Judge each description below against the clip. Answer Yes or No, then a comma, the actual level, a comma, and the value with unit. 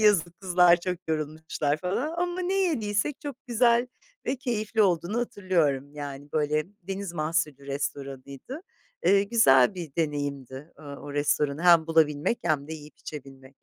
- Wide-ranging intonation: Yes, wide, 6.2 semitones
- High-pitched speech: No, medium, 165 Hz